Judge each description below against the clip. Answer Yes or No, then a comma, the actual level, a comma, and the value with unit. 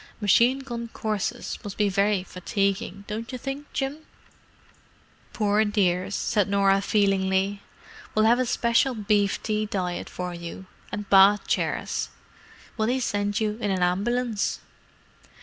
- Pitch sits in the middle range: No, high, 205 Hz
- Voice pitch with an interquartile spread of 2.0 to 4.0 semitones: Yes, average, 2.7 semitones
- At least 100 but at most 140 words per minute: Yes, slow, 135 wpm